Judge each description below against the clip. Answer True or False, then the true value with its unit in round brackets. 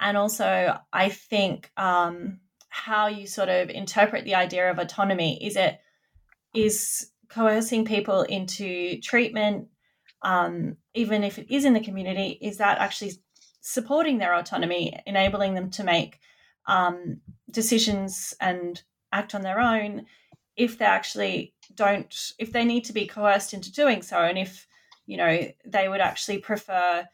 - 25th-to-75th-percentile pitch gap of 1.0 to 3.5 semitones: True (2.9 semitones)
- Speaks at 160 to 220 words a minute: False (150 wpm)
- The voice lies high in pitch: True (205 Hz)